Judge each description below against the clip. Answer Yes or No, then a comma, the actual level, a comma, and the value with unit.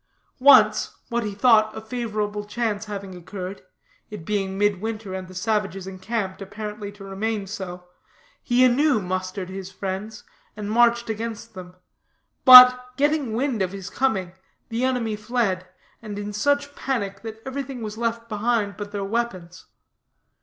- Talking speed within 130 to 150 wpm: Yes, average, 145 wpm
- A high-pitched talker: Yes, high, 210 Hz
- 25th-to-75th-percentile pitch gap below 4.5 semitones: Yes, average, 3.4 semitones